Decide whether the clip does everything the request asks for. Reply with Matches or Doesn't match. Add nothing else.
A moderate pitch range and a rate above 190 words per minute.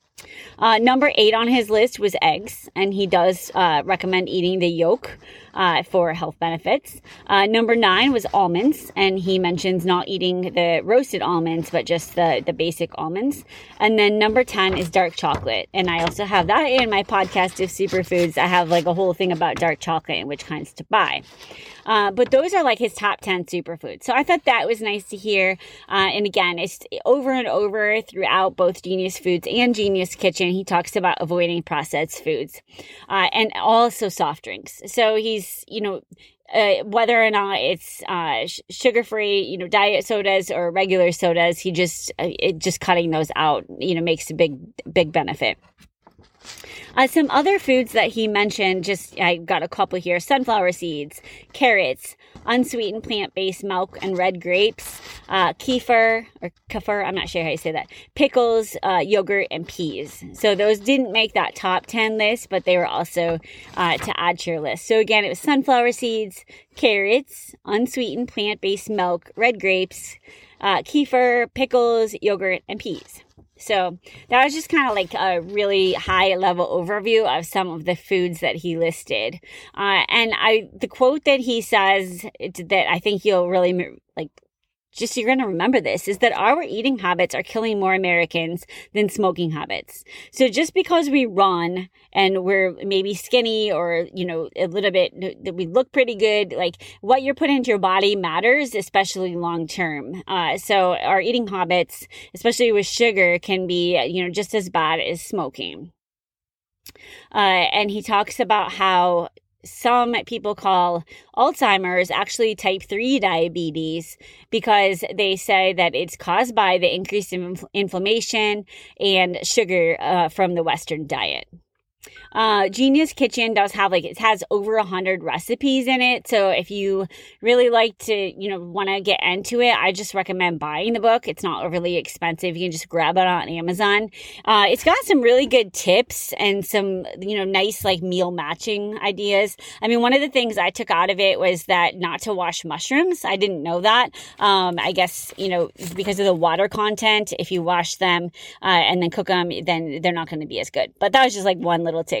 Doesn't match